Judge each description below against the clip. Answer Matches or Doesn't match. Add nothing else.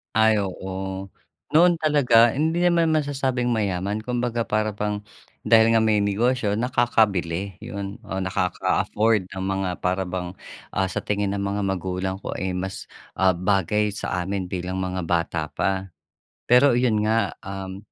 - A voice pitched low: Matches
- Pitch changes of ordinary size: Matches